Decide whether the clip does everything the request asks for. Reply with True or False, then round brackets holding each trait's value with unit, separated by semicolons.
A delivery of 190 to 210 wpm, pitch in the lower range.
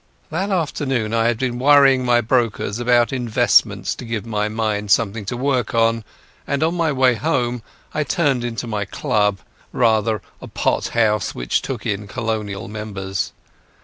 False (155 wpm; 115 Hz)